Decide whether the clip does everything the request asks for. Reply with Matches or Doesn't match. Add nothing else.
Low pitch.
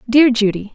Doesn't match